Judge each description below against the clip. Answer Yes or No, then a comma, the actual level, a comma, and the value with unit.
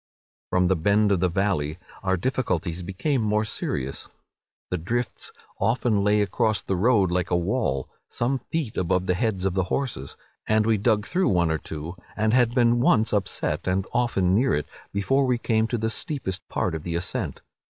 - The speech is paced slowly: No, average, 190 wpm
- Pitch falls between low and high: No, low, 100 Hz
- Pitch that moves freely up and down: No, average, 4.5 semitones